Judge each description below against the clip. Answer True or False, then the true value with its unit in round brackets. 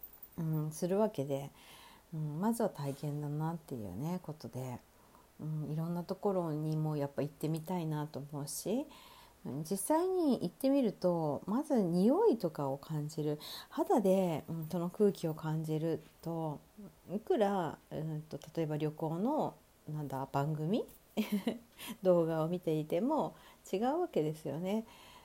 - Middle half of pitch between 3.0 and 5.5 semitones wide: True (5.1 semitones)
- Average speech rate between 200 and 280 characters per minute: True (270 characters per minute)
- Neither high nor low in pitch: True (160 Hz)